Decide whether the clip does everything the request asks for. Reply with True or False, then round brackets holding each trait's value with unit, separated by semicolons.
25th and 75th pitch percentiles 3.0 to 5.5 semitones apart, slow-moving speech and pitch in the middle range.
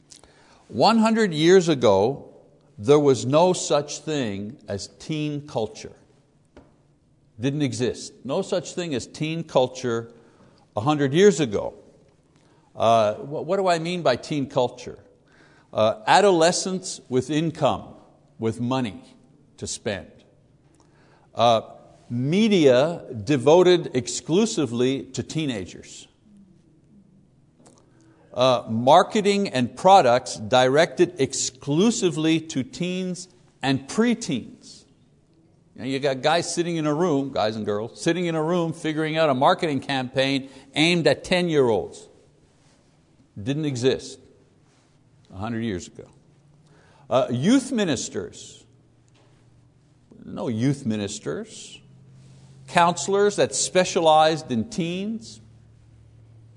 True (5.1 semitones; 100 wpm; 145 Hz)